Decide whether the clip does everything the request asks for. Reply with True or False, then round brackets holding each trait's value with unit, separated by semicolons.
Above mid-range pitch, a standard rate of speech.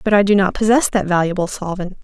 False (195 Hz; 235 wpm)